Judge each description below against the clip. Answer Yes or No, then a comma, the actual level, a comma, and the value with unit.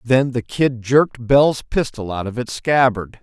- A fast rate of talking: No, average, 185 wpm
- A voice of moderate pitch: No, low, 125 Hz